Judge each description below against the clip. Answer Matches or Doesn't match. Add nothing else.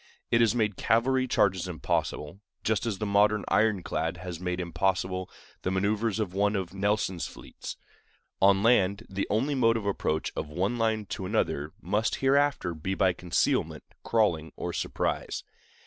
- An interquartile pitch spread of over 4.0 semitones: Doesn't match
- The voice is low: Matches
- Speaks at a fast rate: Doesn't match